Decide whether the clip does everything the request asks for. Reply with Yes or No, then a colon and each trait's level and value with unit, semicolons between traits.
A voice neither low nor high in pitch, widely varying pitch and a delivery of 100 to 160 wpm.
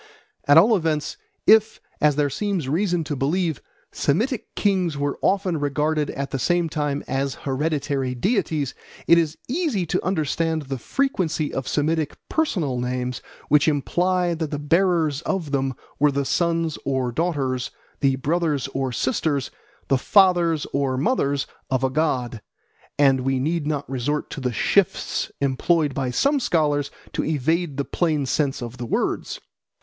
No: medium, 150 Hz; average, 3.9 semitones; average, 155 wpm